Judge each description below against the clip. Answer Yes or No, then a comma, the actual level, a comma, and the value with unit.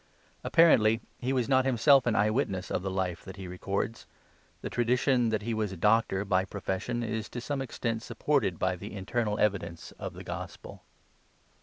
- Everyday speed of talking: Yes, average, 180 wpm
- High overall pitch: No, low, 110 Hz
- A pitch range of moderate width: Yes, average, 4.1 semitones